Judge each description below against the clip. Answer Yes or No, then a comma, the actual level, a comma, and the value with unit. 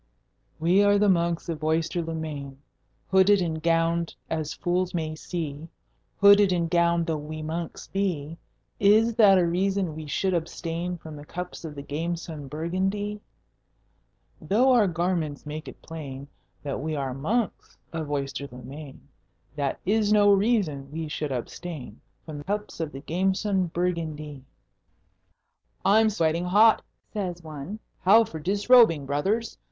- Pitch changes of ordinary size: Yes, average, 4.1 semitones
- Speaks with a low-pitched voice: No, medium, 170 Hz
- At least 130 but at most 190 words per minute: Yes, average, 145 wpm